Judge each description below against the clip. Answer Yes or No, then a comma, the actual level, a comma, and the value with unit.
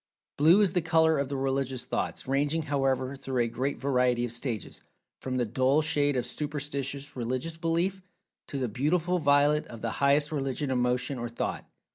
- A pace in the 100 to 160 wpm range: No, average, 175 wpm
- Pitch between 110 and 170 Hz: Yes, medium, 140 Hz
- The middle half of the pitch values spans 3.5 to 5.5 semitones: No, average, 3.0 semitones